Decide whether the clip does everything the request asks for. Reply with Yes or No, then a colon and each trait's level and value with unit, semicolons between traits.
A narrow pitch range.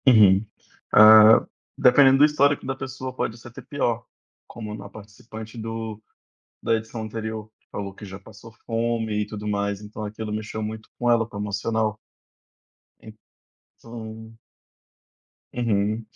Yes: narrow, 1.6 semitones